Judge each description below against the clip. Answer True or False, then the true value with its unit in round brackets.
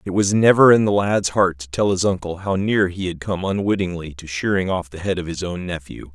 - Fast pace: True (255 wpm)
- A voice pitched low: True (95 Hz)